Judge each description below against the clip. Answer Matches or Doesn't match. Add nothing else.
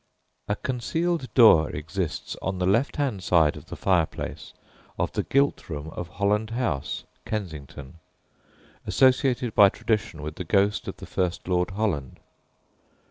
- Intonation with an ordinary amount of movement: Doesn't match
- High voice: Doesn't match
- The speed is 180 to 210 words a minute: Doesn't match